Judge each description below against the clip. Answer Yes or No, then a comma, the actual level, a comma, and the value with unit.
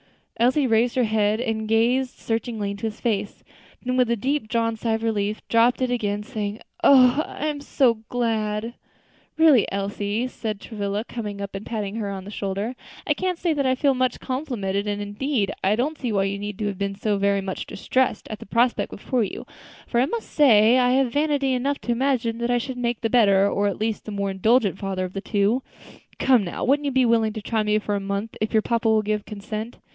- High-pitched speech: Yes, high, 225 Hz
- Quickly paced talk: Yes, fast, 220 wpm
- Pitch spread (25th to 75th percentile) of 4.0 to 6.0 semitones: No, average, 3.6 semitones